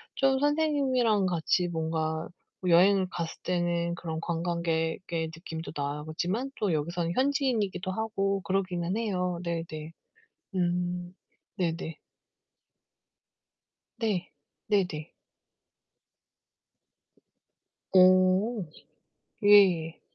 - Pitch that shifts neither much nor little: Yes, average, 3.4 semitones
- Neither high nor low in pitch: Yes, medium, 180 Hz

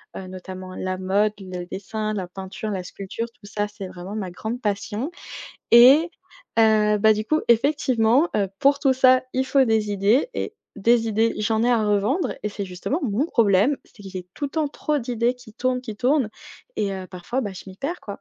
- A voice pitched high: Yes, high, 215 Hz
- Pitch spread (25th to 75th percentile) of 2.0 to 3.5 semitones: No, average, 4.4 semitones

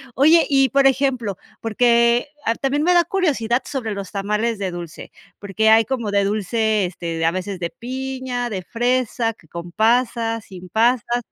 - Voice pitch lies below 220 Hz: No, high, 230 Hz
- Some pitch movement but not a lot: Yes, average, 4.2 semitones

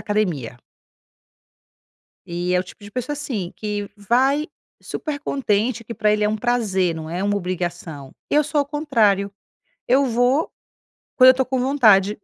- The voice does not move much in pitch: No, wide, 5.4 semitones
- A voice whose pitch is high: Yes, high, 215 Hz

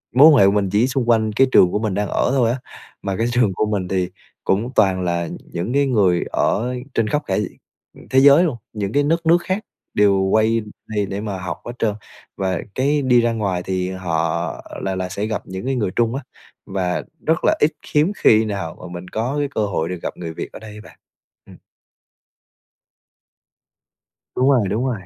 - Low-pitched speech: Yes, low, 110 Hz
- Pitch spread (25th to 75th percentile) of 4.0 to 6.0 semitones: Yes, average, 5.0 semitones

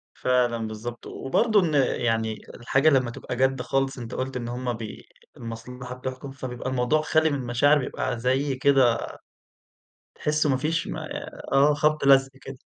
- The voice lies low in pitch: Yes, low, 130 Hz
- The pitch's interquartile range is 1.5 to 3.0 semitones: Yes, narrow, 2.5 semitones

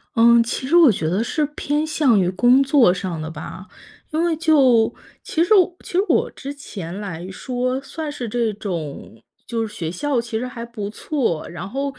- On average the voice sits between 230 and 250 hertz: Yes, high, 235 Hz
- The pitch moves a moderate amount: No, wide, 6.9 semitones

